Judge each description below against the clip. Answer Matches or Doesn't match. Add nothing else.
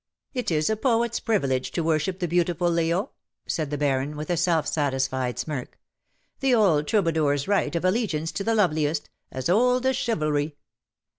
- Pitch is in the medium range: Matches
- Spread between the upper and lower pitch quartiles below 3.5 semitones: Doesn't match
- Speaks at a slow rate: Doesn't match